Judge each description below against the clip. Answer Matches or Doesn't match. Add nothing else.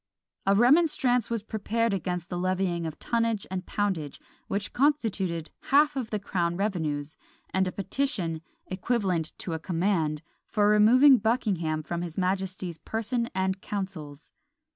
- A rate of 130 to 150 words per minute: Matches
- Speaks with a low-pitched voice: Doesn't match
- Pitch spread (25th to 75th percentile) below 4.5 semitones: Doesn't match